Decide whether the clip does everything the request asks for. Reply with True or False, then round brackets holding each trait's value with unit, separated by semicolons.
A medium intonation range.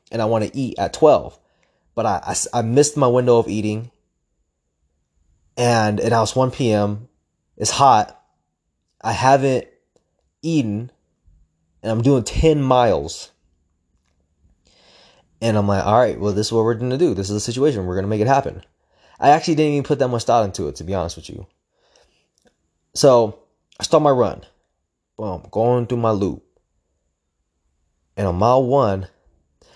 False (7.0 semitones)